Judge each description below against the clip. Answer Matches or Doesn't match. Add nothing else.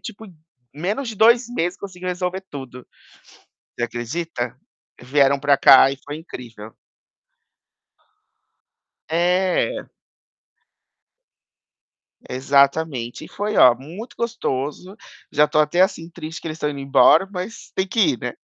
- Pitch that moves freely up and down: Matches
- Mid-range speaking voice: Matches